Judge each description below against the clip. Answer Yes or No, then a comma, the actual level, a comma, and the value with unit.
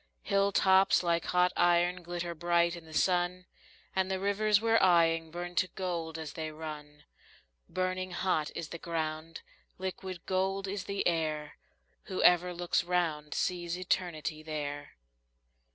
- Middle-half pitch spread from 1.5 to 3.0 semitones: Yes, narrow, 2.4 semitones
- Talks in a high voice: No, medium, 175 Hz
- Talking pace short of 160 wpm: Yes, average, 140 wpm